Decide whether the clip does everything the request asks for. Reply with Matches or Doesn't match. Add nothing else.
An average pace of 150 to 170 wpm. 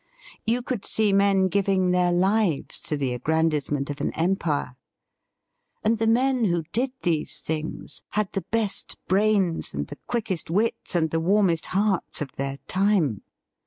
Matches